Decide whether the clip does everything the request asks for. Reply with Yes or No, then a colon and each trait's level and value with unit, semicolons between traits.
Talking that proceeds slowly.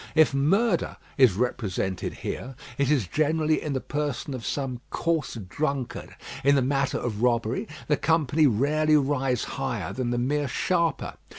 No: average, 155 wpm